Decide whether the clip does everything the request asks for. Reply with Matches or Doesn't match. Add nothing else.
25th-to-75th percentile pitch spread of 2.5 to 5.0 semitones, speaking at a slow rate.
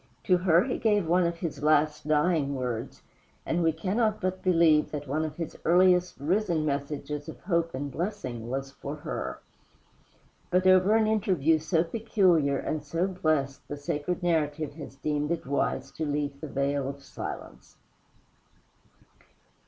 Doesn't match